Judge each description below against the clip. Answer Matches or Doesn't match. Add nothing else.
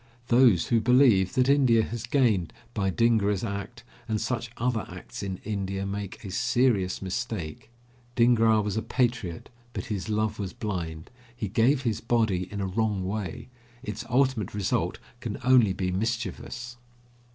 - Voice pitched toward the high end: Doesn't match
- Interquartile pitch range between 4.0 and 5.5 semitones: Doesn't match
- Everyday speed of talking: Matches